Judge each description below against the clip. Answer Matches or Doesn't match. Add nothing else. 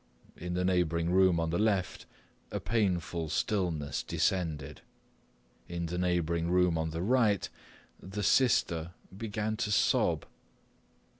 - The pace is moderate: Doesn't match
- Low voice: Matches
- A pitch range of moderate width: Matches